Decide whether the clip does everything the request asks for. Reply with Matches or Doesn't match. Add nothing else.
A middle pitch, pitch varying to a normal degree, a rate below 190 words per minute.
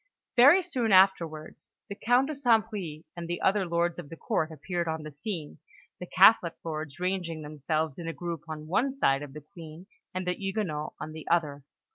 Doesn't match